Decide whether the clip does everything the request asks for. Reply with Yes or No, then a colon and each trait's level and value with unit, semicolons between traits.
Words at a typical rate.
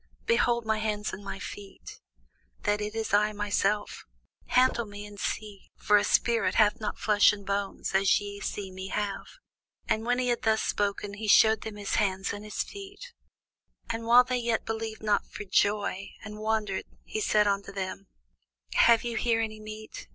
Yes: average, 180 wpm